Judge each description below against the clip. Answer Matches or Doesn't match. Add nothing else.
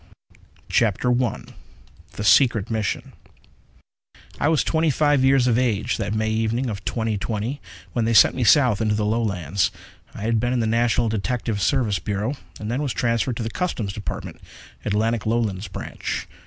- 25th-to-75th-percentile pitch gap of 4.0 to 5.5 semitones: Doesn't match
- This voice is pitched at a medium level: Doesn't match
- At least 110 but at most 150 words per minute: Doesn't match